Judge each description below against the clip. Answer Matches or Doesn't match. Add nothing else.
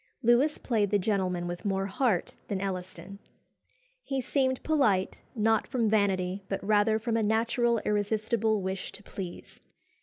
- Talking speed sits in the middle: Matches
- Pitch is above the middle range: Matches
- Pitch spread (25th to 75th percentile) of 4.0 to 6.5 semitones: Doesn't match